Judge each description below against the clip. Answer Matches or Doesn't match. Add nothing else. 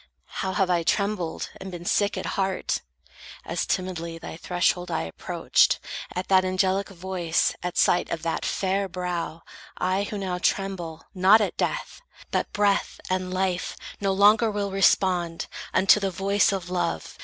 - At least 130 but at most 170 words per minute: Matches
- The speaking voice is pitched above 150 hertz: Matches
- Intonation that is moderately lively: Doesn't match